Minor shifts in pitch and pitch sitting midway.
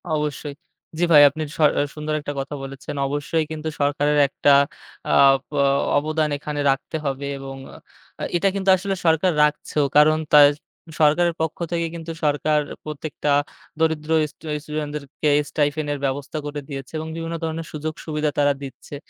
Yes: narrow, 1.6 semitones; medium, 150 Hz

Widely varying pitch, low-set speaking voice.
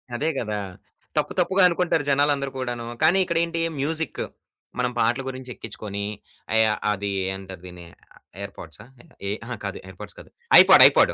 Yes: wide, 7.2 semitones; low, 120 Hz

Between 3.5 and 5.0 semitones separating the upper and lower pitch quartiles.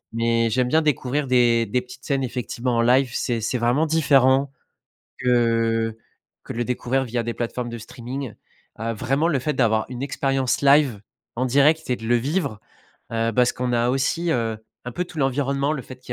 No: average, 2.7 semitones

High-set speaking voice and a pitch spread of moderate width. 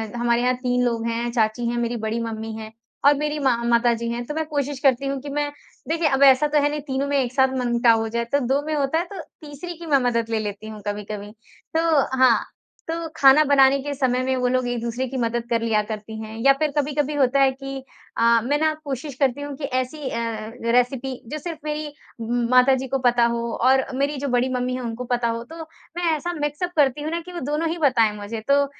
Yes: very high, 260 Hz; average, 3.6 semitones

